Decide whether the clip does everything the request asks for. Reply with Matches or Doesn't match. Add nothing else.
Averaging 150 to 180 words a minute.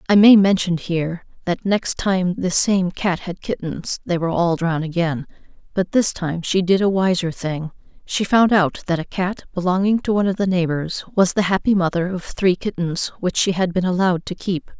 Doesn't match